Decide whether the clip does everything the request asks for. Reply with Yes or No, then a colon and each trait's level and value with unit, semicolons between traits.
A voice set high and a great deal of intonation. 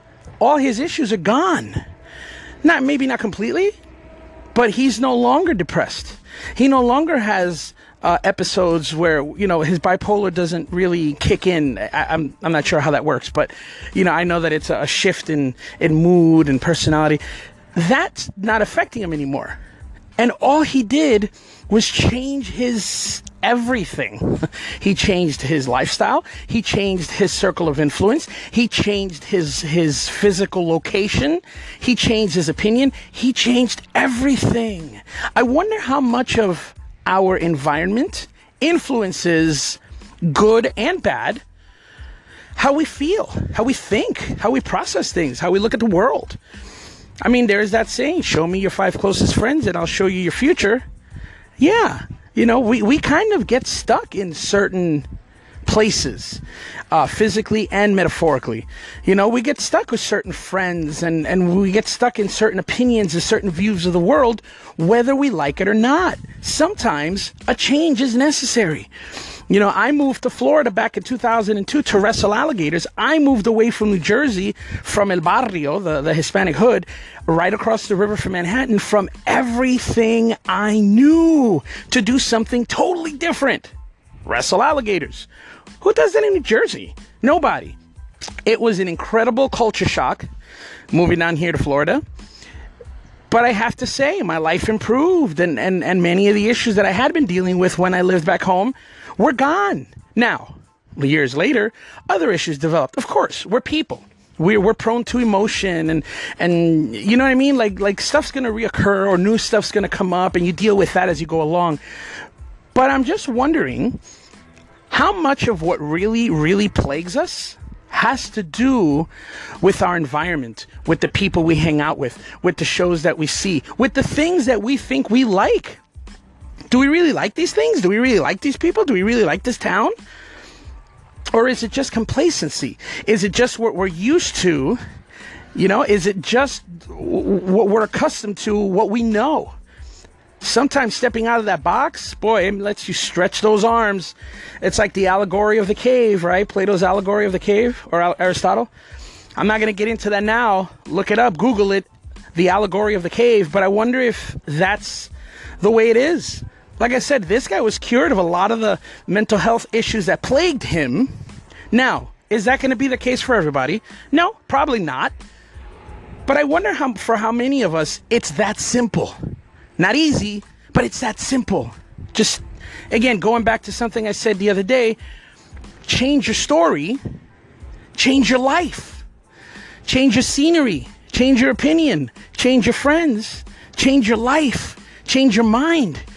Yes: high, 215 Hz; wide, 5.9 semitones